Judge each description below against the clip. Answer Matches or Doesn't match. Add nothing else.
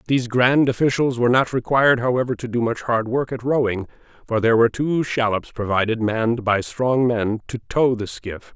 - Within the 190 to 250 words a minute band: Matches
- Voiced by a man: Matches